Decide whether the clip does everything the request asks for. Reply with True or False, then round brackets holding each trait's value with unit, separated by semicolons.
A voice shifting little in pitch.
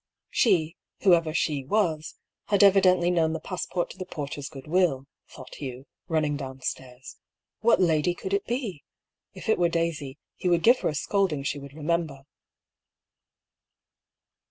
False (4.2 semitones)